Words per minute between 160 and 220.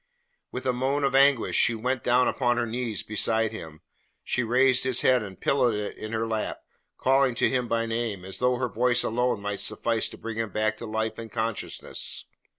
Yes: fast, 205 wpm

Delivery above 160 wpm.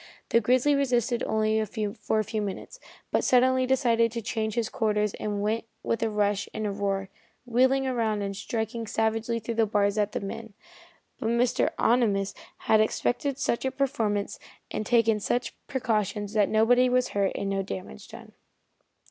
Yes: average, 170 wpm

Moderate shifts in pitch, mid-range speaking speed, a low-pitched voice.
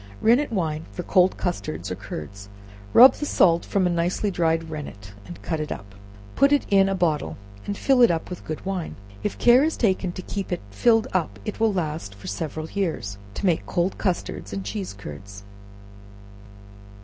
No: average, 4.8 semitones; average, 185 wpm; medium, 175 Hz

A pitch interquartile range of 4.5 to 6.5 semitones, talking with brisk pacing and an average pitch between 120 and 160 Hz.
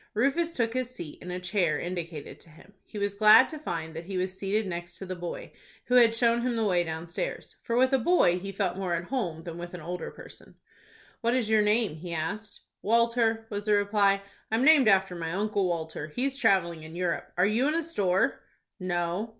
No: average, 4.9 semitones; fast, 215 wpm; high, 195 Hz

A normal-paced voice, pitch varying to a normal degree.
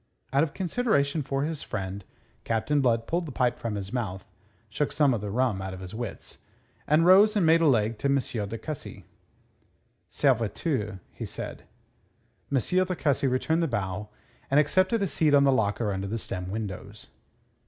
No: average, 180 wpm; wide, 6.6 semitones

